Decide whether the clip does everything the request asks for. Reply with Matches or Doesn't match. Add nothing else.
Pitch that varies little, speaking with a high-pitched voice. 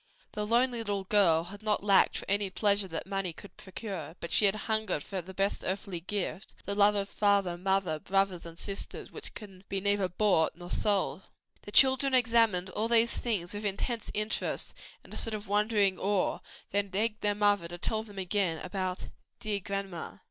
Matches